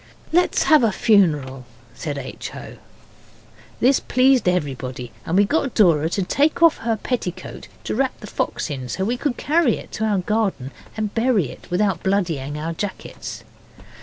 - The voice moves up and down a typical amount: No, wide, 7.9 semitones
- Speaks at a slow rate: No, average, 170 wpm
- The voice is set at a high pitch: Yes, high, 200 Hz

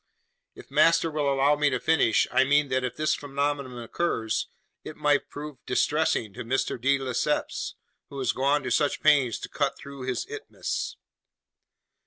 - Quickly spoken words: No, average, 165 wpm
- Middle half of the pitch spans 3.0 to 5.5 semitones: No, narrow, 2.4 semitones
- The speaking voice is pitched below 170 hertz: Yes, medium, 140 Hz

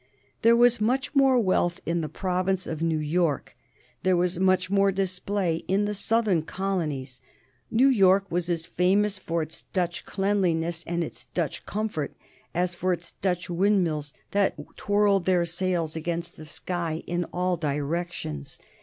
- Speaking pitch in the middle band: Yes, medium, 180 Hz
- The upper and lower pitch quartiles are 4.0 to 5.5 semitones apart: No, average, 2.8 semitones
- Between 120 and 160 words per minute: Yes, average, 155 wpm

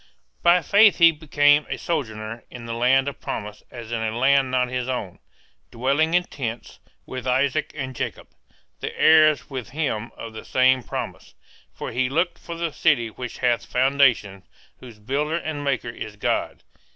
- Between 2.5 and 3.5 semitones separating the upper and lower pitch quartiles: No, average, 4.2 semitones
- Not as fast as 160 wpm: No, average, 170 wpm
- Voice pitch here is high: No, low, 130 Hz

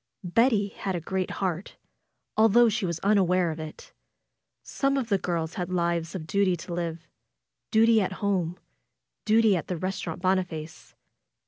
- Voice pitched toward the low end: No, medium, 185 Hz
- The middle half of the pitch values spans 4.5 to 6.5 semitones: No, average, 3.0 semitones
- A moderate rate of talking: Yes, average, 155 wpm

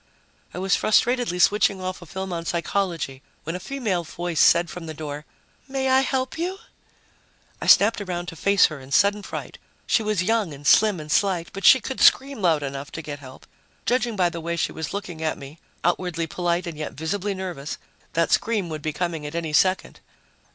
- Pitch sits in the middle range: Yes, medium, 175 Hz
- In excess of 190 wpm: Yes, average, 200 wpm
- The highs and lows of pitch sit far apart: No, average, 4.2 semitones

